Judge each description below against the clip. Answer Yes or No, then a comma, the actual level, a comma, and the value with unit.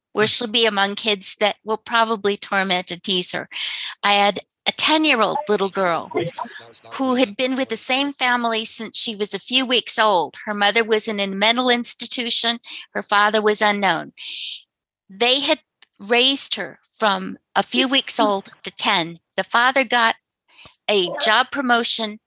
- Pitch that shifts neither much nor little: Yes, average, 3.3 semitones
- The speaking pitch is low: No, high, 220 Hz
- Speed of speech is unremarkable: Yes, average, 165 wpm